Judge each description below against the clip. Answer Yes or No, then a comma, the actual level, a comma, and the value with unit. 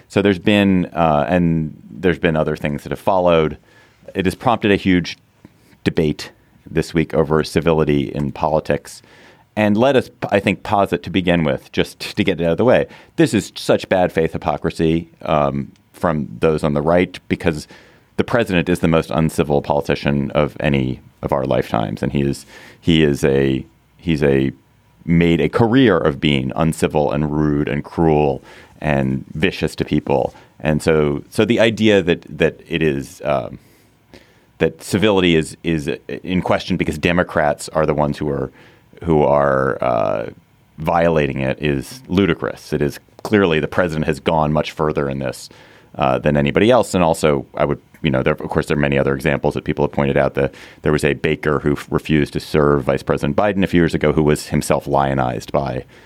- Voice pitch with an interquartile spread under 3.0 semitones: No, average, 3.3 semitones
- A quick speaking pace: No, average, 185 wpm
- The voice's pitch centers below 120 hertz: Yes, very low, 80 Hz